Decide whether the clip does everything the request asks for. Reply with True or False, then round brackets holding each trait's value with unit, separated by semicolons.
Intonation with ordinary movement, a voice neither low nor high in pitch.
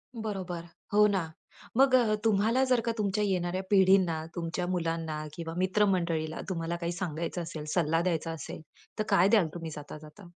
True (3.6 semitones; 175 Hz)